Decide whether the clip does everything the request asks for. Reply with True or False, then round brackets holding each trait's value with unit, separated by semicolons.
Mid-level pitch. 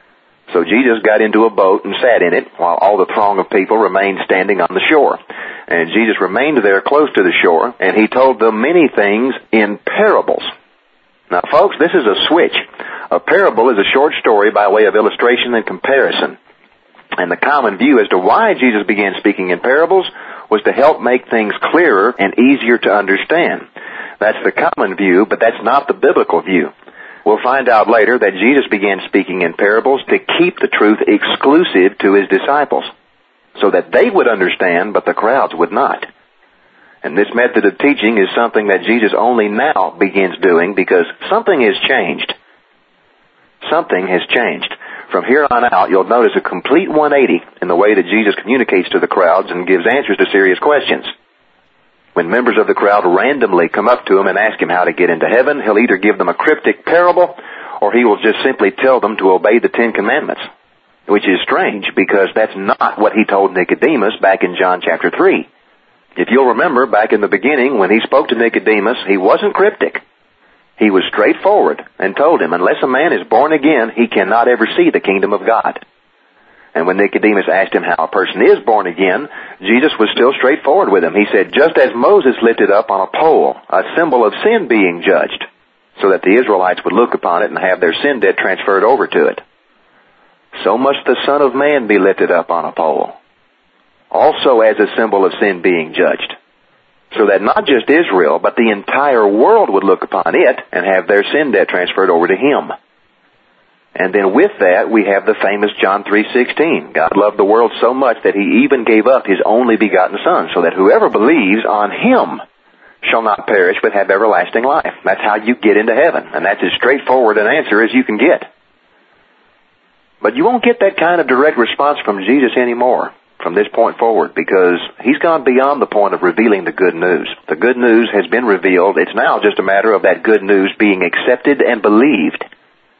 False (120 Hz)